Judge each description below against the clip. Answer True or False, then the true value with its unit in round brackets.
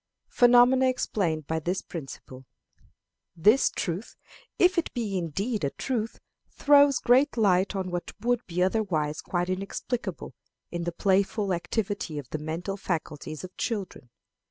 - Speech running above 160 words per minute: False (135 wpm)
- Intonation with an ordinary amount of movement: False (5.7 semitones)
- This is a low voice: False (190 Hz)